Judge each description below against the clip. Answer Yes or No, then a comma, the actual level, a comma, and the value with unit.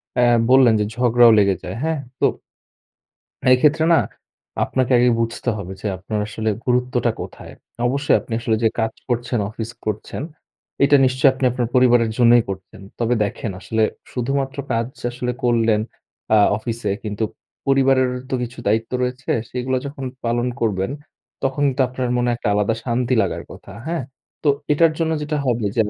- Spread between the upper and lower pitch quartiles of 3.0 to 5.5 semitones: No, narrow, 2.5 semitones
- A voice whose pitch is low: Yes, low, 120 Hz